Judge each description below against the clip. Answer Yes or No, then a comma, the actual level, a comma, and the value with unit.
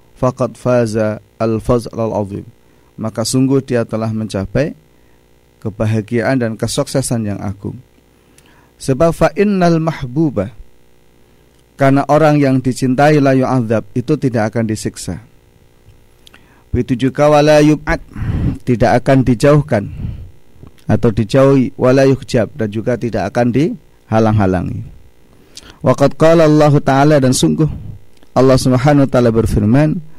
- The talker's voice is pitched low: Yes, low, 120 Hz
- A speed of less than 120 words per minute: Yes, average, 105 wpm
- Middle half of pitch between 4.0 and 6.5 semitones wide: Yes, average, 4.4 semitones